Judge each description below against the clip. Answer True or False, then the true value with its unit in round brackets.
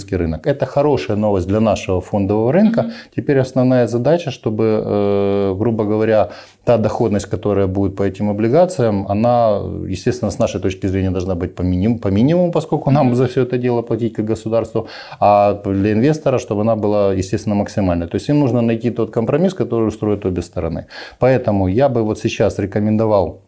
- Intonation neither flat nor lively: True (3.4 semitones)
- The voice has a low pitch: True (110 Hz)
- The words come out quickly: True (165 wpm)